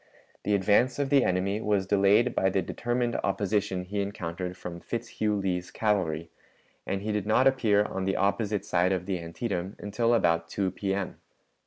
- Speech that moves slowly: No, average, 170 wpm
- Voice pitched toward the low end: Yes, low, 100 Hz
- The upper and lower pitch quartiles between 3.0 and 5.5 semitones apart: No, narrow, 2.6 semitones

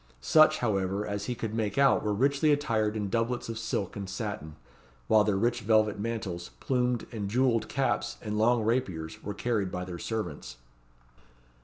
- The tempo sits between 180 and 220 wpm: No, average, 170 wpm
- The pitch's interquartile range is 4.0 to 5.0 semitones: No, average, 3.2 semitones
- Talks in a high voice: No, low, 110 Hz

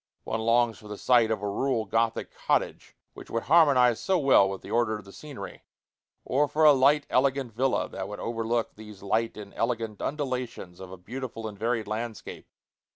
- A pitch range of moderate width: Yes, average, 3.4 semitones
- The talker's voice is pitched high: No, low, 115 Hz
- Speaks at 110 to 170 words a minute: No, average, 190 wpm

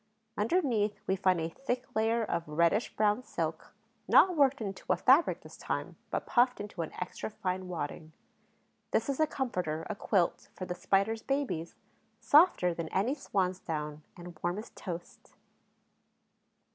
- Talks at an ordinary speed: Yes, average, 155 wpm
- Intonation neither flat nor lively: No, wide, 5.9 semitones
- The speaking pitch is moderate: No, high, 195 Hz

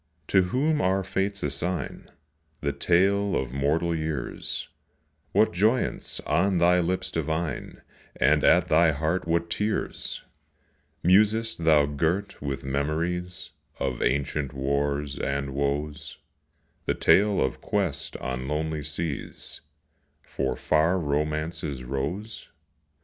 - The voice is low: Yes, very low, 80 Hz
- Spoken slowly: Yes, slow, 110 wpm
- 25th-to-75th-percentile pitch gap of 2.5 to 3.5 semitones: No, average, 4.4 semitones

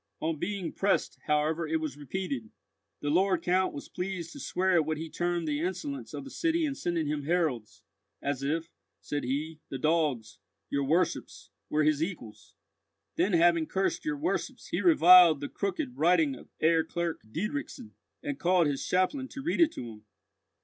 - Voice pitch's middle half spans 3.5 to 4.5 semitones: Yes, average, 4.0 semitones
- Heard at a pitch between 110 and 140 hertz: No, medium, 170 Hz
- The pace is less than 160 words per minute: No, average, 175 wpm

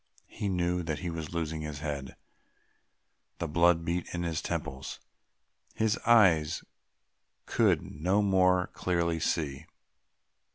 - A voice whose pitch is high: No, very low, 85 Hz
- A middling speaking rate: No, slow, 120 wpm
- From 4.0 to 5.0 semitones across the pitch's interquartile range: No, average, 2.7 semitones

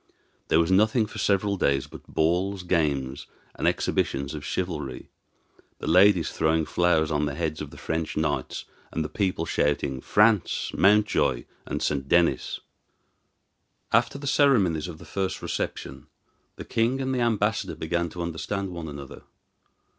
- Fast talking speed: No, average, 150 wpm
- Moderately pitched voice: No, very low, 85 Hz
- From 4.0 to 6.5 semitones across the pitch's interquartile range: Yes, average, 4.6 semitones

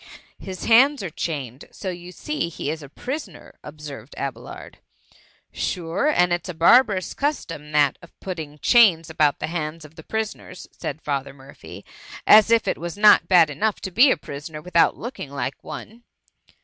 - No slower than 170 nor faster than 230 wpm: Yes, average, 190 wpm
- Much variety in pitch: Yes, wide, 5.8 semitones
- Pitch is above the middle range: No, medium, 170 Hz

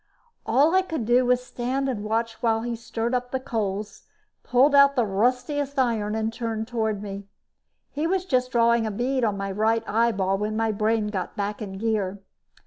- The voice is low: No, high, 230 Hz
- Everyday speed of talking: Yes, average, 190 wpm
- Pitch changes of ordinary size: Yes, average, 3.0 semitones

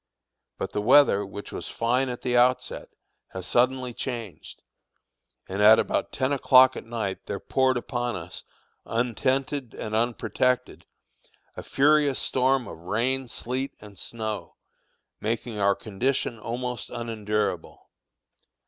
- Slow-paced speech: Yes, slow, 120 wpm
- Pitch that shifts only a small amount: No, average, 3.4 semitones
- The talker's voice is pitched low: Yes, low, 120 Hz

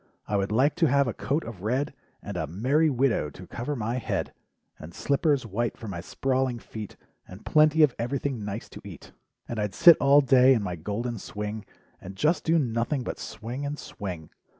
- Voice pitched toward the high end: No, low, 120 Hz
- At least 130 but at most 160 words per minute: No, average, 195 wpm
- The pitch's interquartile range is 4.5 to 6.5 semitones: Yes, average, 5.2 semitones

